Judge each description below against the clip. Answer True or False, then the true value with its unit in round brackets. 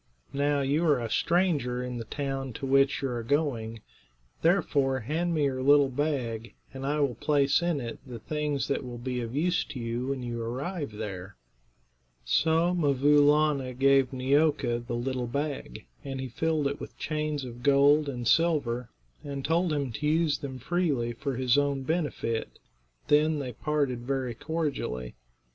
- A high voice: False (140 Hz)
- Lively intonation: False (3.4 semitones)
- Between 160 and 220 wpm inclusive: True (170 wpm)